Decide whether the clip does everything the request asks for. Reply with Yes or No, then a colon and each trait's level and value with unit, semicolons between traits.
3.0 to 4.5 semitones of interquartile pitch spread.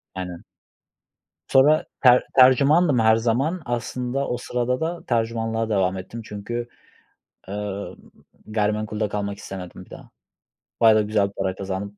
Yes: average, 3.6 semitones